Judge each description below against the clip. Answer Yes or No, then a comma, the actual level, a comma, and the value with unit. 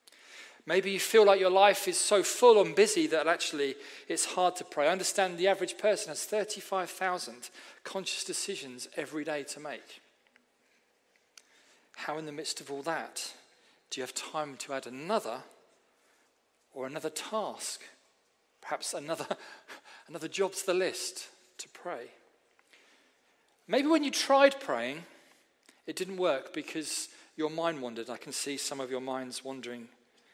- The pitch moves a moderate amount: No, wide, 5.9 semitones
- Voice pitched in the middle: Yes, medium, 170 Hz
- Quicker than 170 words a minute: No, average, 150 wpm